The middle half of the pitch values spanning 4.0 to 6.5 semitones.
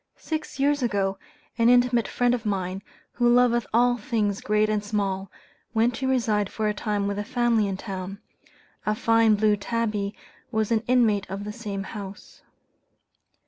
No: average, 2.9 semitones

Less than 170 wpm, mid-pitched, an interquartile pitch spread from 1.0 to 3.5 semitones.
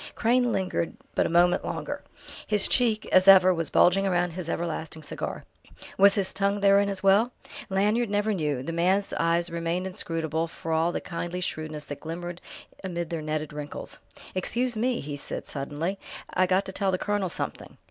No: average, 180 wpm; medium, 180 Hz; average, 3.2 semitones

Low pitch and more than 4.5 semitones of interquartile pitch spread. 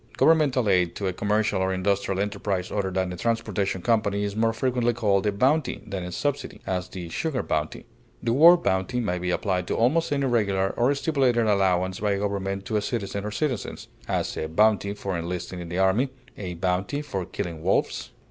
No: low, 100 Hz; average, 4.0 semitones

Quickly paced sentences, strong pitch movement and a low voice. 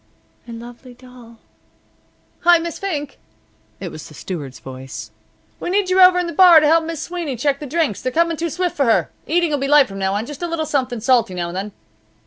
No: fast, 235 wpm; wide, 6.6 semitones; very high, 285 Hz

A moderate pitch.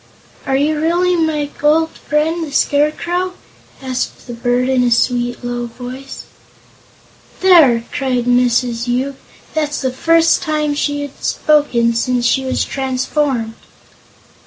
No: very high, 270 Hz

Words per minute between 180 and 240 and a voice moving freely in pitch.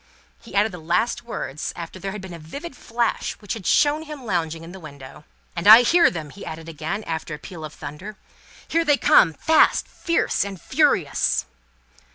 Yes: average, 195 wpm; wide, 6.6 semitones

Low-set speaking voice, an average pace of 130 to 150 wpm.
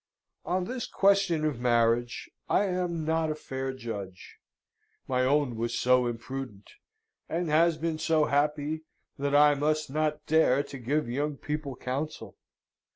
No: medium, 145 Hz; average, 145 wpm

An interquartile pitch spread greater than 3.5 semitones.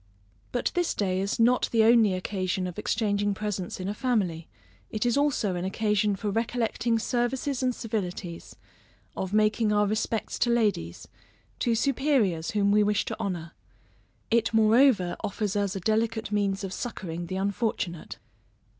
No: average, 3.2 semitones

